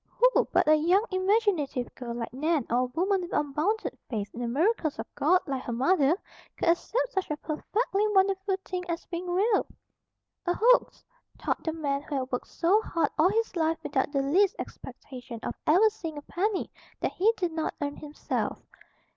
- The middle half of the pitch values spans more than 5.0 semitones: Yes, wide, 5.5 semitones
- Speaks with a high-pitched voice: Yes, very high, 335 Hz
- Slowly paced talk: No, average, 190 wpm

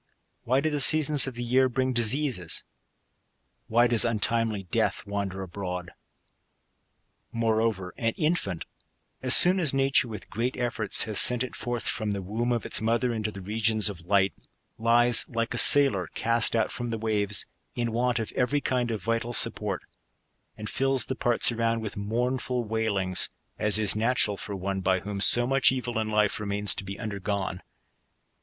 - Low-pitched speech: Yes, low, 115 Hz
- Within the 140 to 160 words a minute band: No, average, 175 wpm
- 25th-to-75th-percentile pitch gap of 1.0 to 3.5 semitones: Yes, average, 3.1 semitones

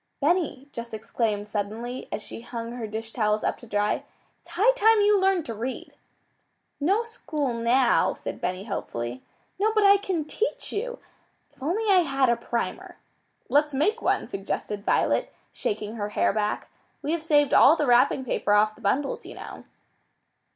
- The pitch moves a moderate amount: No, wide, 8.0 semitones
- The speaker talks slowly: No, average, 170 wpm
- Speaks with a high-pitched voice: Yes, very high, 255 Hz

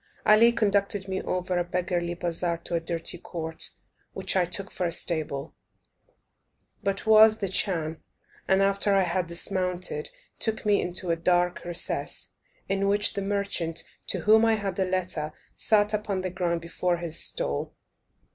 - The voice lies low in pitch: No, medium, 185 Hz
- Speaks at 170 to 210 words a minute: No, average, 160 wpm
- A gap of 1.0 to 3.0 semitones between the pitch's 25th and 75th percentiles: Yes, average, 2.7 semitones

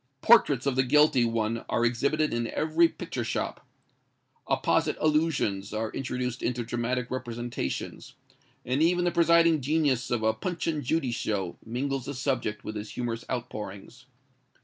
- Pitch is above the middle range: No, low, 125 Hz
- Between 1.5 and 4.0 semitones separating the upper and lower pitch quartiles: No, average, 4.6 semitones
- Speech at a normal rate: Yes, average, 150 wpm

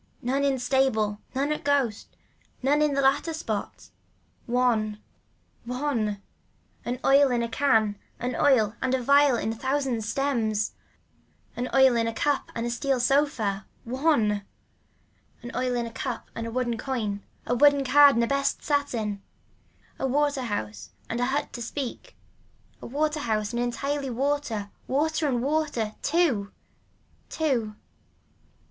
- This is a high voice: Yes, very high, 250 Hz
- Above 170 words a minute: No, average, 150 wpm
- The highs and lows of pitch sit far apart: No, average, 3.9 semitones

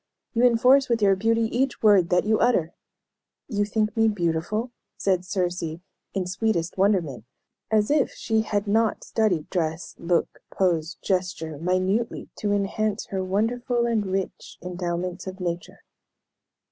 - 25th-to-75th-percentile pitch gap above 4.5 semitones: No, average, 3.7 semitones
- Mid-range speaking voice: No, high, 195 Hz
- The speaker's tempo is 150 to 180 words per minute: No, average, 140 wpm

